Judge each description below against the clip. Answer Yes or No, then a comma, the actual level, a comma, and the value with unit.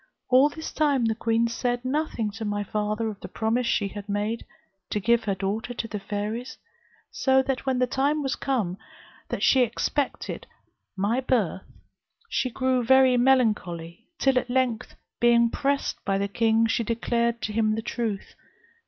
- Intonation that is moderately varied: Yes, average, 3.4 semitones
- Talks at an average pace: Yes, average, 170 wpm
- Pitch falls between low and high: No, high, 235 Hz